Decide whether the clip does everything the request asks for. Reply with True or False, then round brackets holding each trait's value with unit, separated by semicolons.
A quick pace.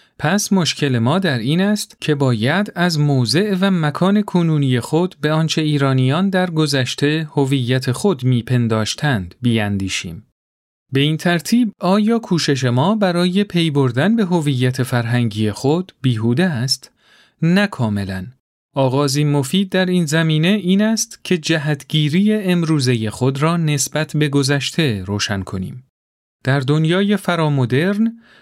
False (125 wpm)